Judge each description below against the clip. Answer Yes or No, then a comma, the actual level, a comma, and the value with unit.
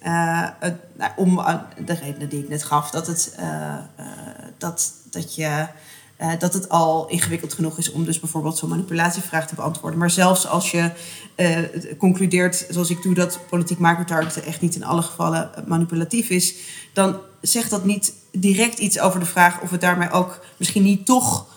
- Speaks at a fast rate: No, average, 185 wpm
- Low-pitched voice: No, medium, 170 Hz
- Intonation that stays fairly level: Yes, narrow, 1.9 semitones